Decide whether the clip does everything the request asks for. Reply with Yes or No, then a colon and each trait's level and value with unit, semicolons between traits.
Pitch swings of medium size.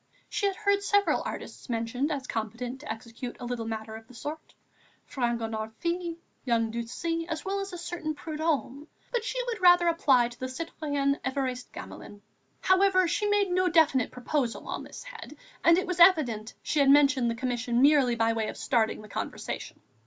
No: wide, 6.6 semitones